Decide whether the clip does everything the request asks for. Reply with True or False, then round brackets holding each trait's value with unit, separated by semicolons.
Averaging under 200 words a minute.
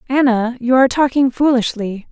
True (140 wpm)